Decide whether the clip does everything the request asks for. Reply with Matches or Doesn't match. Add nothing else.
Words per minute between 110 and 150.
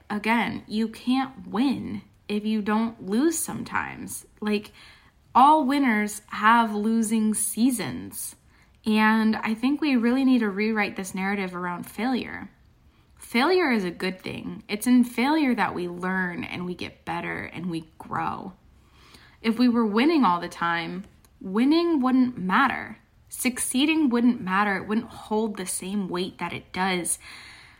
Matches